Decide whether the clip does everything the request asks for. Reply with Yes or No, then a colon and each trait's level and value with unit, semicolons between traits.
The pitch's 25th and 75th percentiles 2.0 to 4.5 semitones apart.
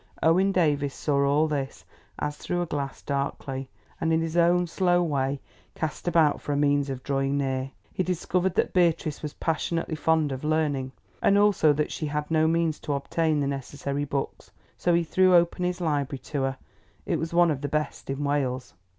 Yes: average, 3.1 semitones